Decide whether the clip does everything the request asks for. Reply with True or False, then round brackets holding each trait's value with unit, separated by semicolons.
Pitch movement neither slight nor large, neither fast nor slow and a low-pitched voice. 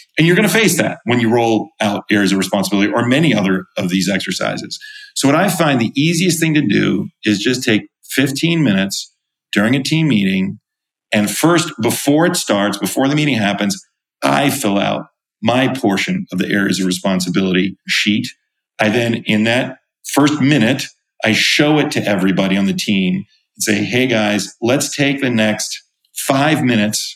False (7.5 semitones; 180 wpm; 120 Hz)